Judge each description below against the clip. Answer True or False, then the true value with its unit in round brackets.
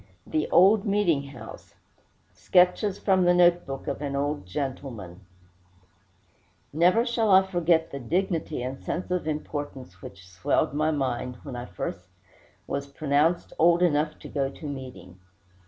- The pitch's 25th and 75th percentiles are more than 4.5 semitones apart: True (4.9 semitones)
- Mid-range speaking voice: True (150 Hz)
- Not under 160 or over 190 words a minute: False (145 wpm)